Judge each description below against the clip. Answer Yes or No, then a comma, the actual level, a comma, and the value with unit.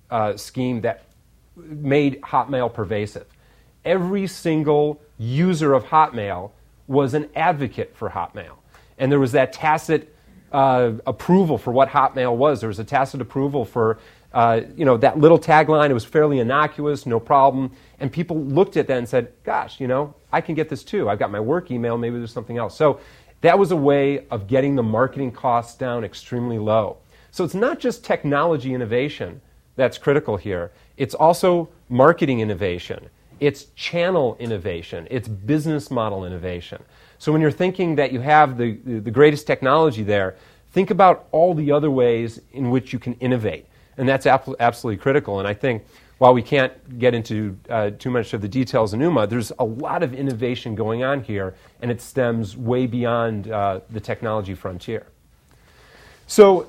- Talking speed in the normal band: Yes, average, 180 wpm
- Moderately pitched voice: No, low, 130 Hz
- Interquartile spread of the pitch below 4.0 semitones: No, average, 4.4 semitones